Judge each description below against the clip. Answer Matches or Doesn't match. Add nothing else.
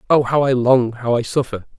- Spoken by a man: Matches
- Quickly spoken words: Matches